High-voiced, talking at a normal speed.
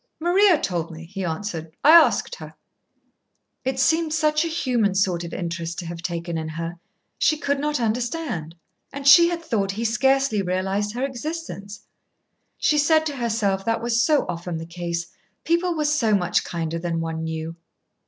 Yes: high, 210 Hz; average, 175 wpm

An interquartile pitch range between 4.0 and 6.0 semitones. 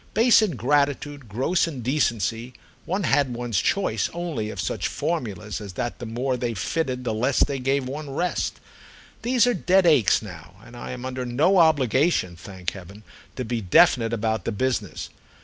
Yes: average, 5.2 semitones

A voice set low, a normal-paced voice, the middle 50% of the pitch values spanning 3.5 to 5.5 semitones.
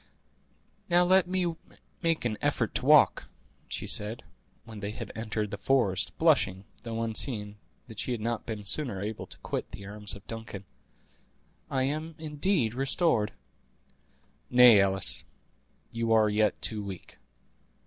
Yes: low, 115 Hz; average, 145 wpm; average, 4.7 semitones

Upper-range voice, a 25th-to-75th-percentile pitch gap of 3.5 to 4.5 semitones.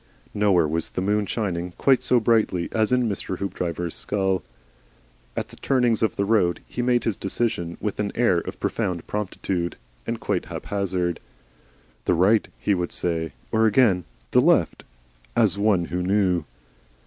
No: low, 100 Hz; average, 3.8 semitones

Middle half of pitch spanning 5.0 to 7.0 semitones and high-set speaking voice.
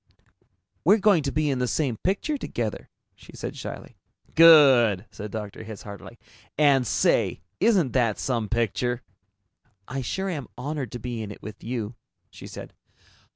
No: wide, 5.4 semitones; low, 125 Hz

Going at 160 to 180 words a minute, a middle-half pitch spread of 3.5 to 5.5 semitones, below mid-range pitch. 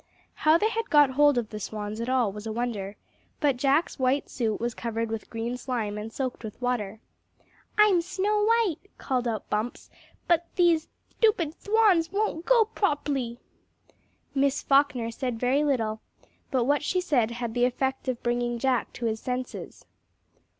No: average, 165 wpm; average, 5.1 semitones; very high, 255 Hz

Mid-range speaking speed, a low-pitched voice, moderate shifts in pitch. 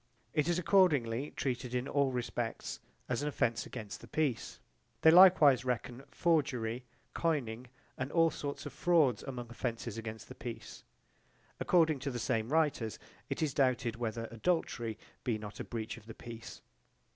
Yes: average, 155 wpm; low, 125 Hz; average, 4.5 semitones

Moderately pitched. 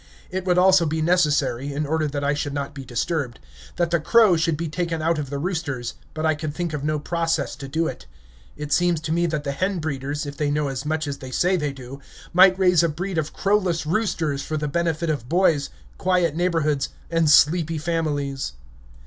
Yes: medium, 155 Hz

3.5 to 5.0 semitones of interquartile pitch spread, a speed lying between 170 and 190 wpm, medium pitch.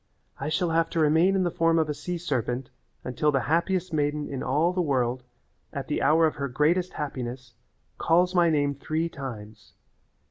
Yes: average, 3.8 semitones; average, 185 wpm; medium, 150 Hz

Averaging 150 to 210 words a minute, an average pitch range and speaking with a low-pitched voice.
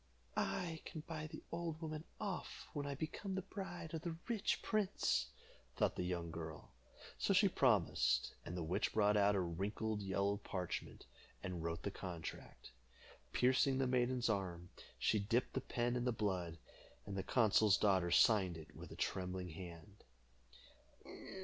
No: average, 160 wpm; wide, 8.1 semitones; low, 105 Hz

